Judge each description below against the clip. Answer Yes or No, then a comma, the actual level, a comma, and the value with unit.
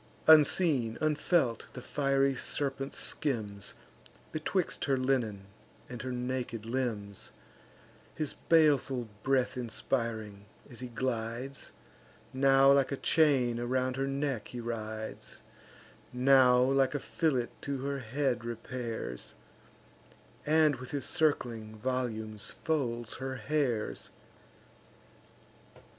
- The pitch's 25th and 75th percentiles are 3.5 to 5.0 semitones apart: No, average, 2.9 semitones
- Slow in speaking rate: Yes, slow, 105 wpm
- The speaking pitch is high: No, low, 130 Hz